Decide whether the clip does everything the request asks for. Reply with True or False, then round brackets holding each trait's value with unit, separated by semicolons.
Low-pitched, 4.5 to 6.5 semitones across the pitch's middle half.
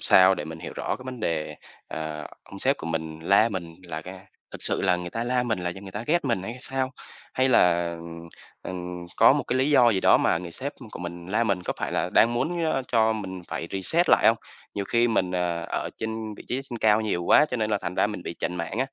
True (95 Hz; 5.2 semitones)